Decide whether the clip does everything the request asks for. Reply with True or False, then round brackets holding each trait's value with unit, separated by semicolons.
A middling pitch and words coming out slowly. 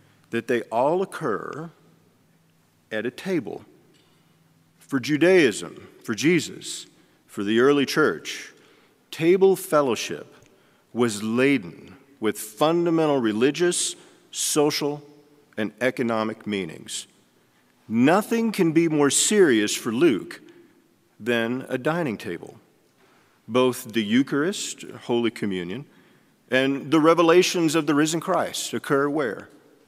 True (145 Hz; 100 wpm)